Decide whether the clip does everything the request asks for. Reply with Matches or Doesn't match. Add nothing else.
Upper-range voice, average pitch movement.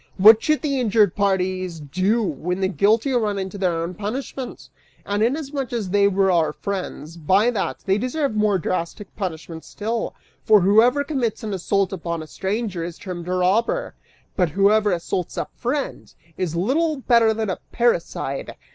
Matches